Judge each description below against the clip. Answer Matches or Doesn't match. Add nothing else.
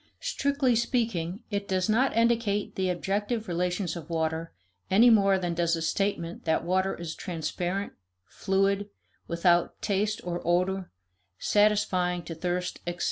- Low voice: Doesn't match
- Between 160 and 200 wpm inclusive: Doesn't match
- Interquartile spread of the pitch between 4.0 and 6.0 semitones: Doesn't match